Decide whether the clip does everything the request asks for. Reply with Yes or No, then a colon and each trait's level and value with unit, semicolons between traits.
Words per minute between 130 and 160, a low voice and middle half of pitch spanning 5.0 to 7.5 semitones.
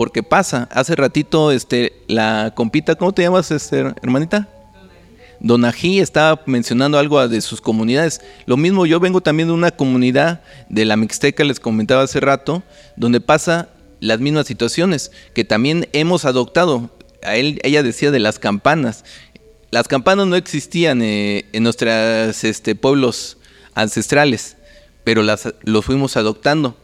Yes: average, 145 wpm; low, 130 Hz; average, 5.3 semitones